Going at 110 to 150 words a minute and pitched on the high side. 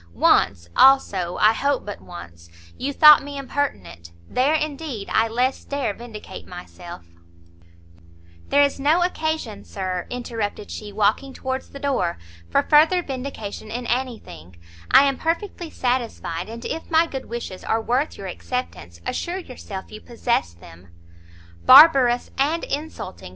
Yes: average, 145 wpm; high, 240 Hz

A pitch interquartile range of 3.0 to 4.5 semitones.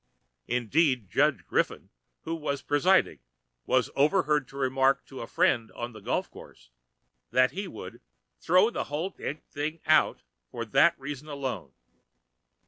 Yes: average, 3.9 semitones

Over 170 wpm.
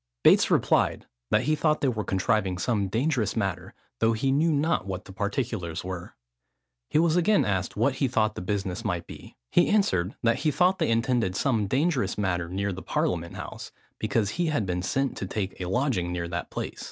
Yes: average, 200 wpm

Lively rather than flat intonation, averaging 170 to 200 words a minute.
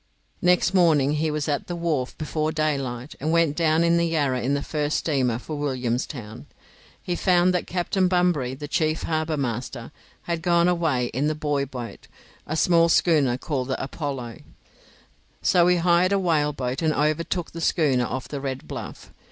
No: average, 4.1 semitones; average, 175 wpm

